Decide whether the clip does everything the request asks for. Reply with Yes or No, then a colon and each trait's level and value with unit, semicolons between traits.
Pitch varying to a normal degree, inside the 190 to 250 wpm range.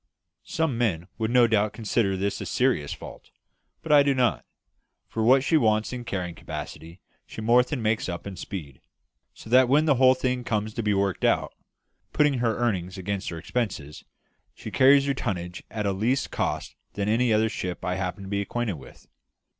Yes: average, 4.5 semitones; average, 195 wpm